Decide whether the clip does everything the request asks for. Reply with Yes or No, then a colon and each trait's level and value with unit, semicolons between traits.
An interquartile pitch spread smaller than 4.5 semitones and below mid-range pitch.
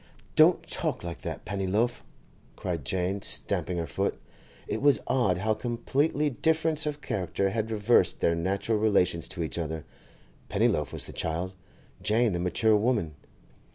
No: average, 5.2 semitones; low, 100 Hz